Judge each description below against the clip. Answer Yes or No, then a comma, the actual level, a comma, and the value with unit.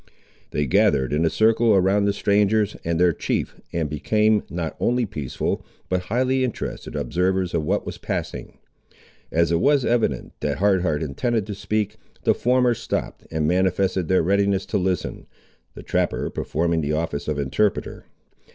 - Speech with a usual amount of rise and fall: Yes, average, 4.6 semitones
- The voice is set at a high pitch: No, very low, 95 Hz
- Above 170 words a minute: No, average, 160 wpm